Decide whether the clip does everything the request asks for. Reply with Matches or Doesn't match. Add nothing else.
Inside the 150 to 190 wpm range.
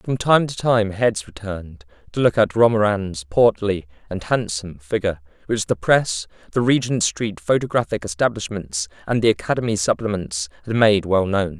Matches